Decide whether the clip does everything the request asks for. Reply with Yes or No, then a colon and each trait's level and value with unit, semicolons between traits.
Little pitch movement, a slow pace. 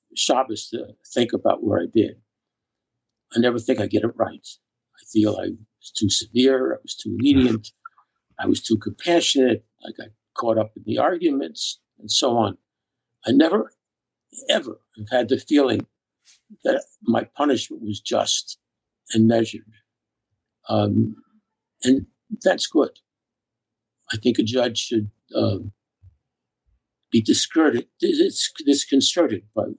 No: average, 3.2 semitones; slow, 130 wpm